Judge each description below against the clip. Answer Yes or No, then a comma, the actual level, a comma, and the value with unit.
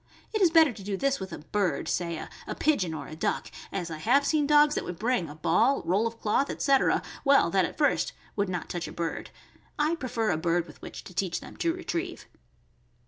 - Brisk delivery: Yes, fast, 225 wpm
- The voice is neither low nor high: No, high, 210 Hz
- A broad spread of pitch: Yes, wide, 8.6 semitones